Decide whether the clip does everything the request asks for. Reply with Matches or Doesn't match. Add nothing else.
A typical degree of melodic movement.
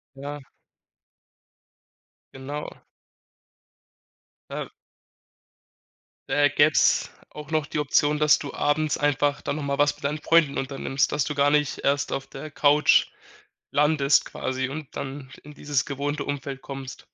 Doesn't match